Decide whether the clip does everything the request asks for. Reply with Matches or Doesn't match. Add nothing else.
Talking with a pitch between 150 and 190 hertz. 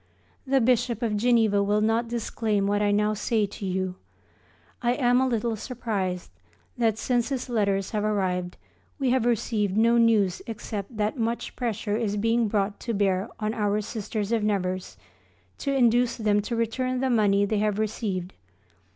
Doesn't match